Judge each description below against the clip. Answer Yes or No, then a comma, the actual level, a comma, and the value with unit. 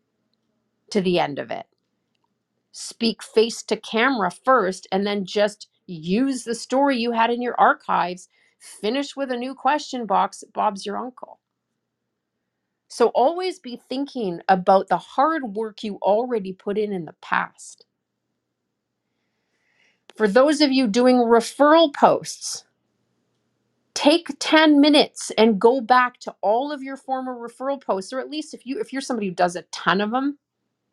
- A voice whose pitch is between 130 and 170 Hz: No, high, 235 Hz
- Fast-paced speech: No, average, 150 wpm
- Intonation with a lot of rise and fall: No, average, 4.6 semitones